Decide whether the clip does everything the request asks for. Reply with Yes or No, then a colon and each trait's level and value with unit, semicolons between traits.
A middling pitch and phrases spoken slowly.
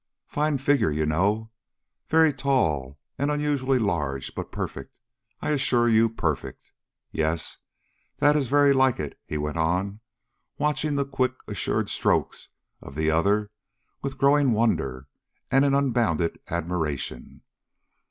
No: low, 115 Hz; slow, 130 wpm